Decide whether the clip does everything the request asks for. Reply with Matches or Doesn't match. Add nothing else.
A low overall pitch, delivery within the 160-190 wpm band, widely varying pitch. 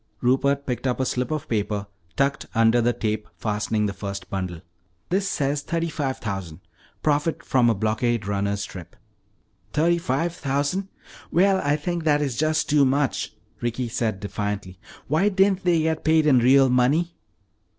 Matches